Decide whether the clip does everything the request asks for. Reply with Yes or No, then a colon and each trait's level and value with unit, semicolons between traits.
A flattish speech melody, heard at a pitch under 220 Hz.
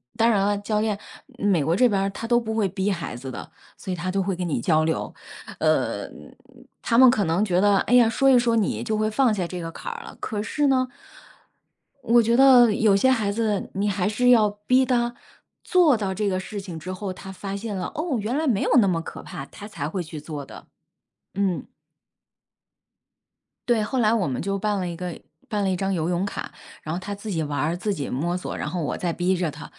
No: average, 4.0 semitones; high, 200 Hz